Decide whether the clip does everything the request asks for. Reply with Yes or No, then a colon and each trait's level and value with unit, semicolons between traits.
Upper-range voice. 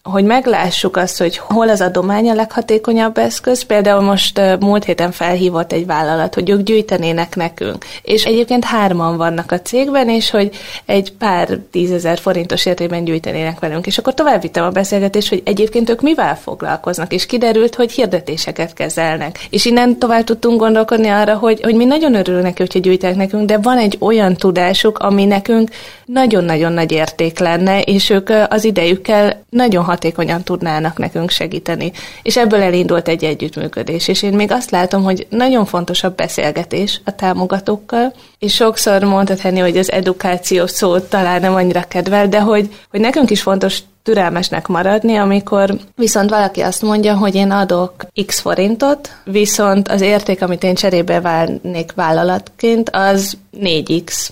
Yes: high, 195 Hz